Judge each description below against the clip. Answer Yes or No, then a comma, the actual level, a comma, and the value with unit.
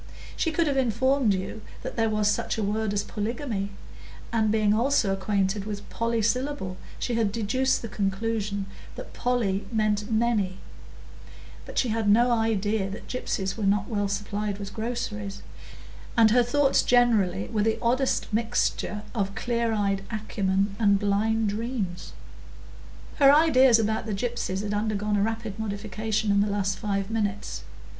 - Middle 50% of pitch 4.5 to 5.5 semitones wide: No, narrow, 2.5 semitones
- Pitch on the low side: No, high, 215 Hz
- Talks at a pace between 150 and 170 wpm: Yes, average, 155 wpm